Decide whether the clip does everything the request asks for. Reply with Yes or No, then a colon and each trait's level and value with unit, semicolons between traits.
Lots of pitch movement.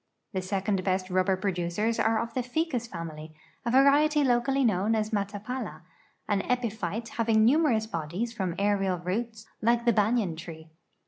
No: average, 4.2 semitones